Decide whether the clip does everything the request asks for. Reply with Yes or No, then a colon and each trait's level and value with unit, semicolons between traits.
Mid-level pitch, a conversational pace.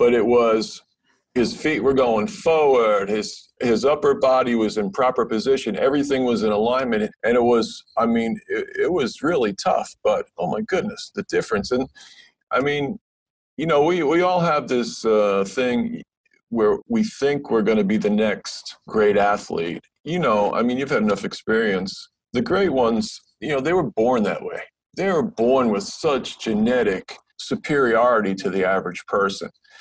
Yes: medium, 145 Hz; average, 175 wpm